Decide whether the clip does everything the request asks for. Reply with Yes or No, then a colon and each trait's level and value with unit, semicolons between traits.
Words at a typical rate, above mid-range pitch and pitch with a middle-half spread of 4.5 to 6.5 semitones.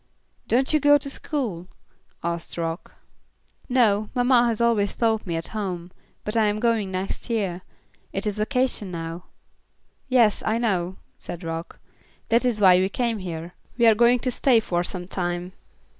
Yes: average, 165 wpm; high, 210 Hz; average, 4.9 semitones